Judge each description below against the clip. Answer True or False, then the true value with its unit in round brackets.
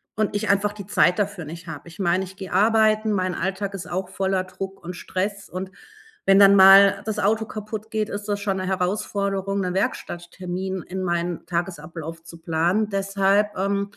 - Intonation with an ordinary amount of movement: False (2.0 semitones)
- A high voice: True (195 Hz)